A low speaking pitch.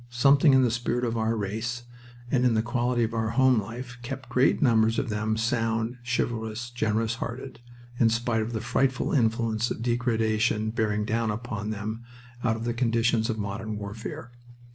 Yes: low, 115 Hz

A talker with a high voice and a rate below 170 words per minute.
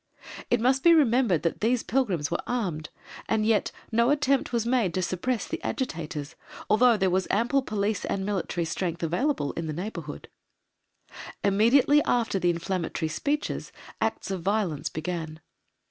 Yes: high, 205 Hz; average, 150 wpm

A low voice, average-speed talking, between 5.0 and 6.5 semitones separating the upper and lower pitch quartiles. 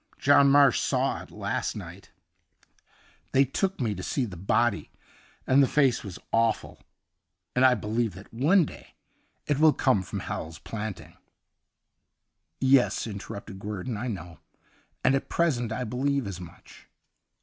Yes: low, 120 Hz; average, 160 wpm; average, 5.3 semitones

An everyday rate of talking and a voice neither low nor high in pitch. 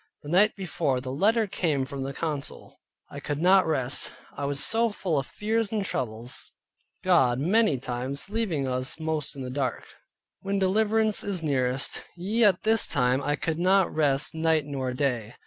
Yes: average, 175 wpm; medium, 155 Hz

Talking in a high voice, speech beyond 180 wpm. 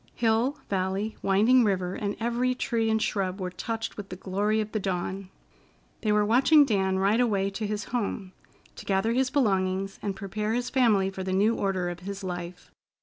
Yes: high, 205 Hz; average, 190 wpm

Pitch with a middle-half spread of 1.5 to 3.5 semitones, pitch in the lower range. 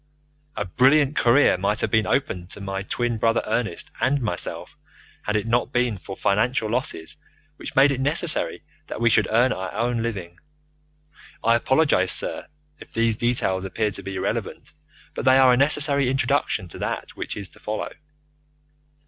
No: average, 4.8 semitones; low, 115 Hz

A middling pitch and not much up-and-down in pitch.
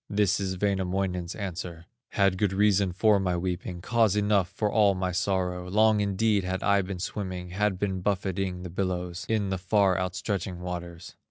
No: very low, 95 Hz; narrow, 2.0 semitones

